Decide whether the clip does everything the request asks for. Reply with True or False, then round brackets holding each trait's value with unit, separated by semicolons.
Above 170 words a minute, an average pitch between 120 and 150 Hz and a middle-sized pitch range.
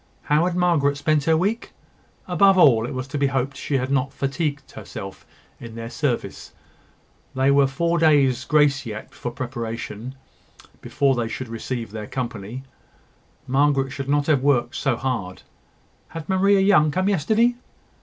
False (155 wpm; 140 Hz; 3.8 semitones)